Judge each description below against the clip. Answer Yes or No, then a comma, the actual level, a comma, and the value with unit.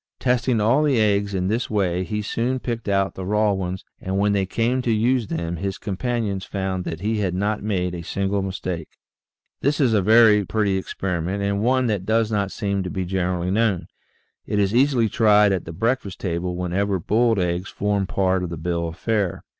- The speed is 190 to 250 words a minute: Yes, average, 200 wpm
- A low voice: Yes, low, 100 Hz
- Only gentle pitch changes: No, average, 3.1 semitones